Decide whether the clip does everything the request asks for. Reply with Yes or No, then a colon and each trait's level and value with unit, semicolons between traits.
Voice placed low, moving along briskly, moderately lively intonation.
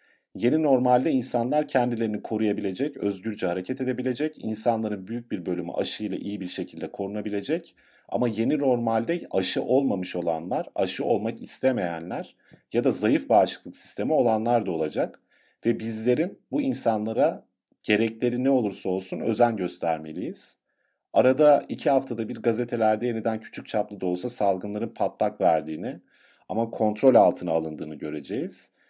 No: low, 115 Hz; average, 130 wpm; average, 3.3 semitones